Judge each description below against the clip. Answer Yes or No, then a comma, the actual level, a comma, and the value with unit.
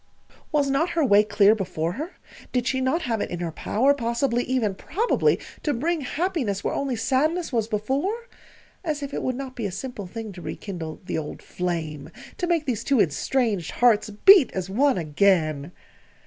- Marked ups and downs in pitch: Yes, wide, 6.5 semitones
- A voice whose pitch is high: Yes, high, 235 Hz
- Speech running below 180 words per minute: No, average, 190 wpm